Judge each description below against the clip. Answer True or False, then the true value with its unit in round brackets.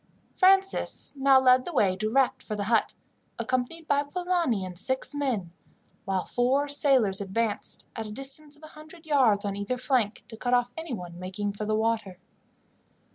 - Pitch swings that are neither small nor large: False (5.7 semitones)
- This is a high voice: True (245 Hz)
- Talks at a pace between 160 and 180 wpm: True (170 wpm)